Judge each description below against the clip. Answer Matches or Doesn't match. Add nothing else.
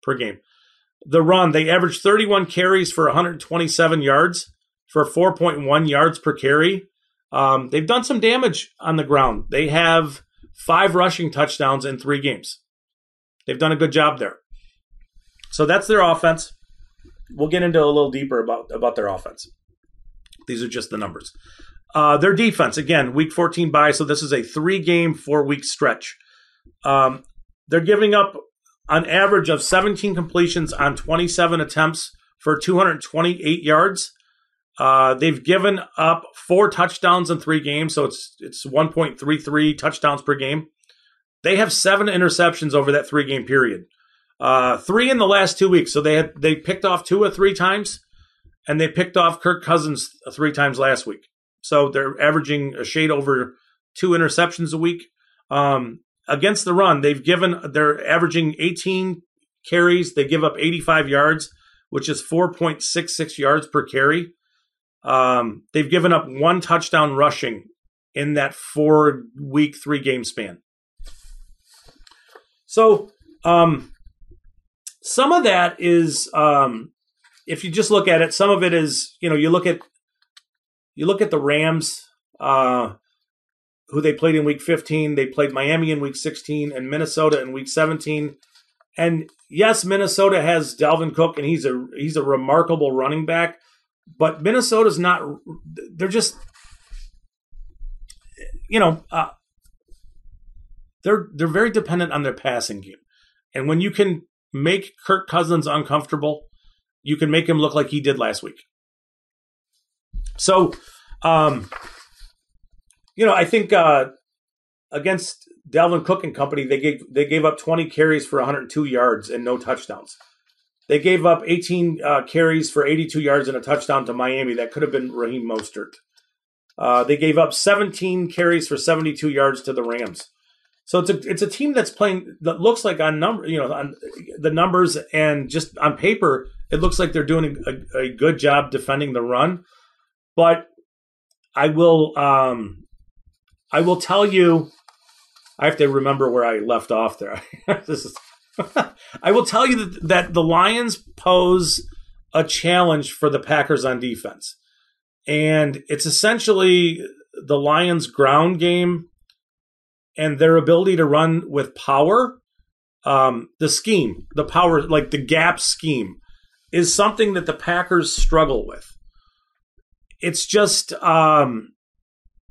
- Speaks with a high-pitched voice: Doesn't match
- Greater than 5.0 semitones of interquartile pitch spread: Doesn't match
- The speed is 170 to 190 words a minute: Doesn't match